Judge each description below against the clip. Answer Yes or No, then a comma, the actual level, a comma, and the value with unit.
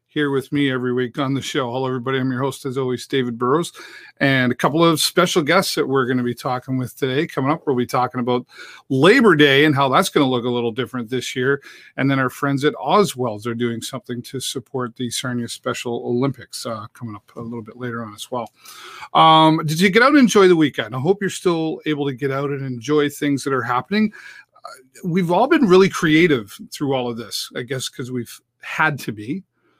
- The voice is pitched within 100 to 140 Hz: Yes, low, 135 Hz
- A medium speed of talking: No, fast, 230 wpm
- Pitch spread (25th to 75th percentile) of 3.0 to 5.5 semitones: Yes, average, 3.3 semitones